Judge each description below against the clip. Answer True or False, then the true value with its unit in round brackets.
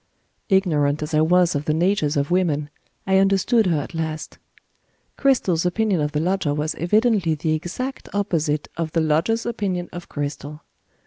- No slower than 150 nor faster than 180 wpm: True (165 wpm)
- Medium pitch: True (170 Hz)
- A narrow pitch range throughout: False (4.1 semitones)